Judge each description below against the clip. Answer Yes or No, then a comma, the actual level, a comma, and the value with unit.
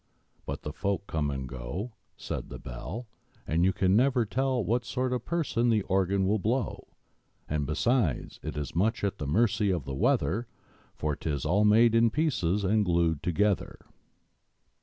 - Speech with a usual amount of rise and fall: No, wide, 6.6 semitones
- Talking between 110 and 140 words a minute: No, average, 170 wpm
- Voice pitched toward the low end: Yes, low, 100 Hz